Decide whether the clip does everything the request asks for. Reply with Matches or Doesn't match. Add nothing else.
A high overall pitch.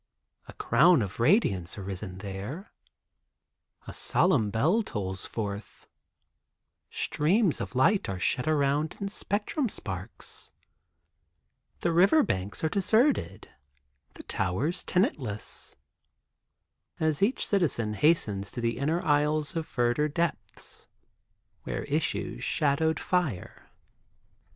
Doesn't match